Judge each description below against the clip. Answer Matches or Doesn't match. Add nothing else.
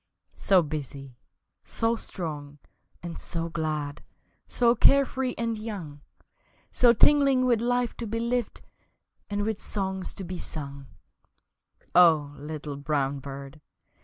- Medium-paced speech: Doesn't match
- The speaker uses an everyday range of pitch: Doesn't match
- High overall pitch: Doesn't match